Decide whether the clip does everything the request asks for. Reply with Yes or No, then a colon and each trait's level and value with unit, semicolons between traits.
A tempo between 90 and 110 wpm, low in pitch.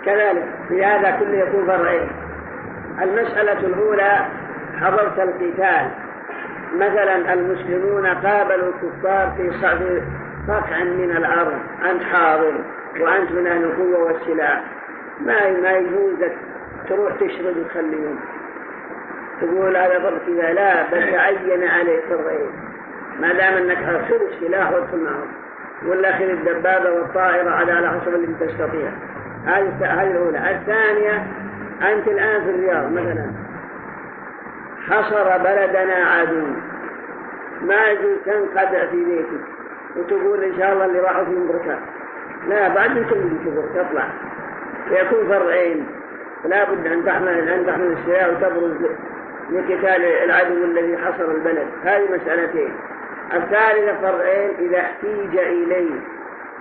No: average, 105 wpm; medium, 185 Hz